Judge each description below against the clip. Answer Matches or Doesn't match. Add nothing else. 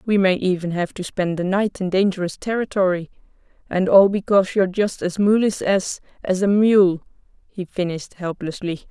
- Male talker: Doesn't match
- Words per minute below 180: Matches